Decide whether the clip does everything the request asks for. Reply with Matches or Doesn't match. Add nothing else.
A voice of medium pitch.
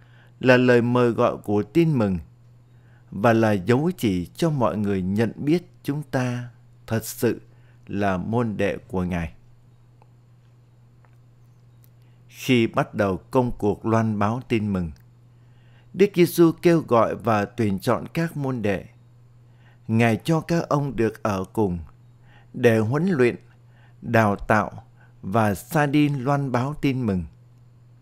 Doesn't match